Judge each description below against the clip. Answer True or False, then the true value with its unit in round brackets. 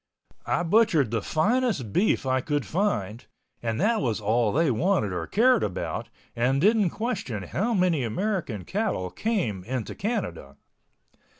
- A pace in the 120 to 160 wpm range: True (140 wpm)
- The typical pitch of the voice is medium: True (145 Hz)